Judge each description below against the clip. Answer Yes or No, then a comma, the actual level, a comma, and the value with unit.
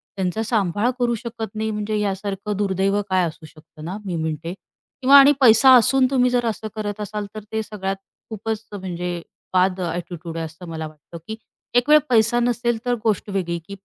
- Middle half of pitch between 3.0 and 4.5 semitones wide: Yes, average, 4.1 semitones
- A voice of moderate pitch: No, high, 205 Hz